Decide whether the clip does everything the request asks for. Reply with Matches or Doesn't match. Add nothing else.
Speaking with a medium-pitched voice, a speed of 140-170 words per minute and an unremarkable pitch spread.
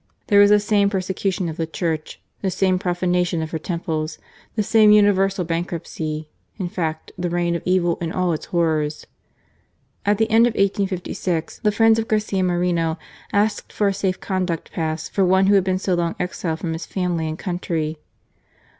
Doesn't match